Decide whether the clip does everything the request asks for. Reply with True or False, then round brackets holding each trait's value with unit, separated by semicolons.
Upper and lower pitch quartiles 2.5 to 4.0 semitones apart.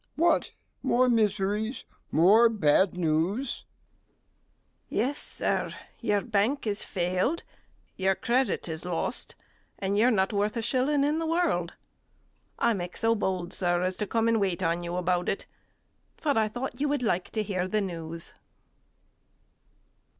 False (4.8 semitones)